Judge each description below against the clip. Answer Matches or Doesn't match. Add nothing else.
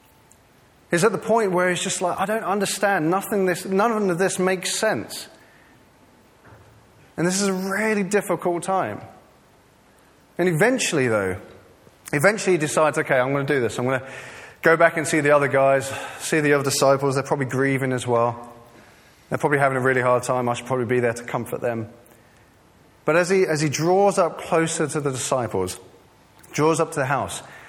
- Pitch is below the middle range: Doesn't match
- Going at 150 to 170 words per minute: Doesn't match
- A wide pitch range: Matches